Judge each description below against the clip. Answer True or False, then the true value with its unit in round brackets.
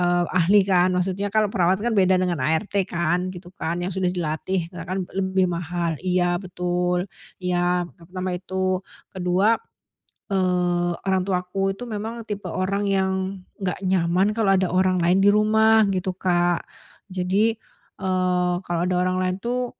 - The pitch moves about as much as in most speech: False (1.5 semitones)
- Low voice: False (185 Hz)